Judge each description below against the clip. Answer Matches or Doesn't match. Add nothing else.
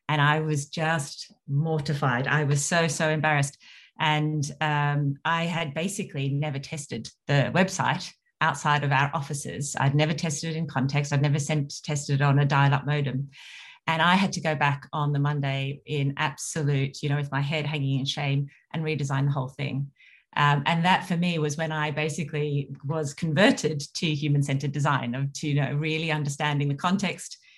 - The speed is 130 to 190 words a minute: Matches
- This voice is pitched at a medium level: Matches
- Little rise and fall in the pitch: Matches